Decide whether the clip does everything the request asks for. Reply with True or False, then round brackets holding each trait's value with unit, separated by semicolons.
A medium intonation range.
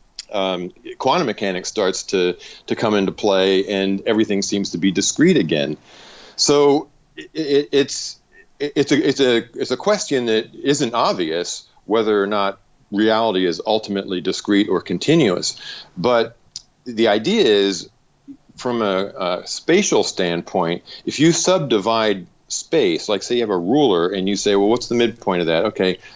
True (4.3 semitones)